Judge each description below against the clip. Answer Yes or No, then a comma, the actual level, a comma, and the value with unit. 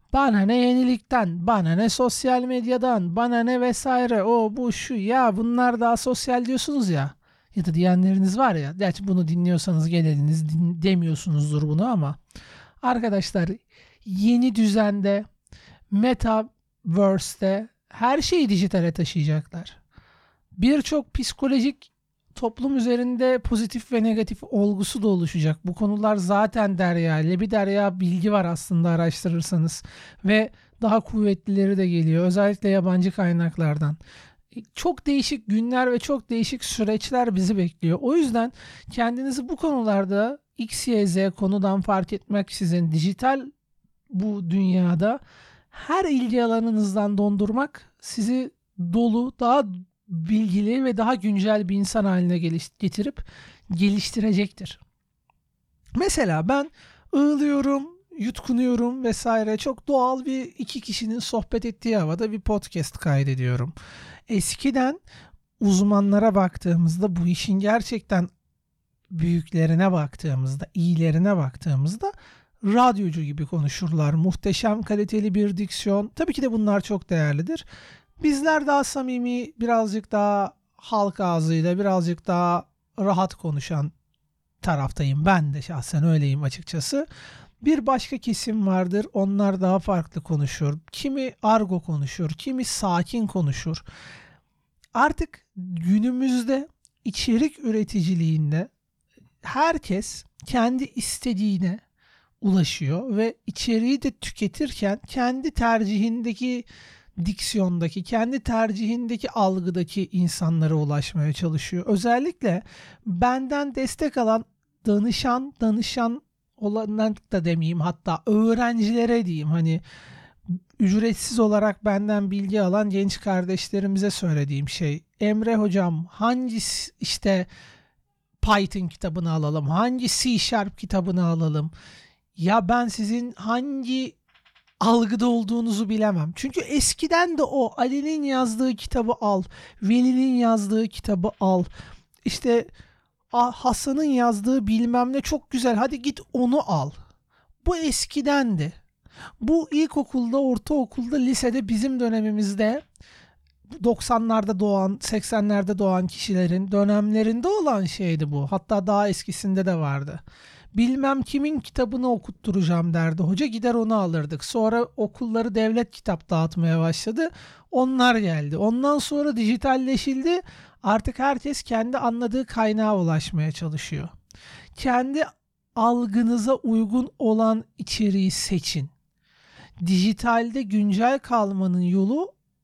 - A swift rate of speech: No, average, 105 wpm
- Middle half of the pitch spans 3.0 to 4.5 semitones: No, average, 5.3 semitones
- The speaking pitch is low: No, high, 210 Hz